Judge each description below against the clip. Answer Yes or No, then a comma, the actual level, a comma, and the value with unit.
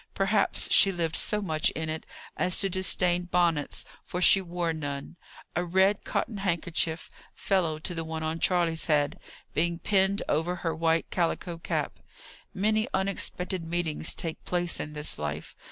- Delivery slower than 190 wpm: Yes, average, 155 wpm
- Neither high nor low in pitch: Yes, medium, 170 Hz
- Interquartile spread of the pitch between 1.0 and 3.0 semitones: Yes, average, 2.7 semitones